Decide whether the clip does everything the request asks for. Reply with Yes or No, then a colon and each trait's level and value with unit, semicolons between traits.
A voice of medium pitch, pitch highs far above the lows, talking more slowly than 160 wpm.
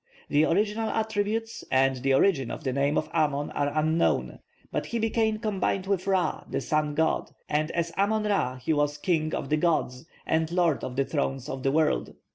No: medium, 155 Hz; wide, 5.8 semitones; average, 195 wpm